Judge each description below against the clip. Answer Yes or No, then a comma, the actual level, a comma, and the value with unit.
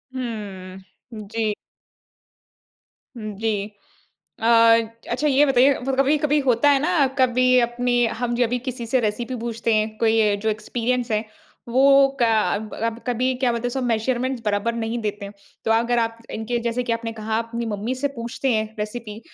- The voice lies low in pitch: No, high, 230 Hz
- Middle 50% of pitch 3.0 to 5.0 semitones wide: No, narrow, 2.4 semitones